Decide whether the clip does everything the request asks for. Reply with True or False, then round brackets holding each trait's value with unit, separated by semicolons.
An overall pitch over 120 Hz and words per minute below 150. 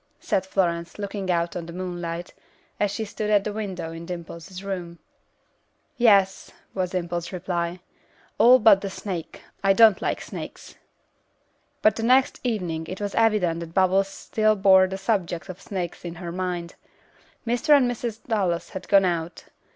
False (190 Hz; 160 wpm)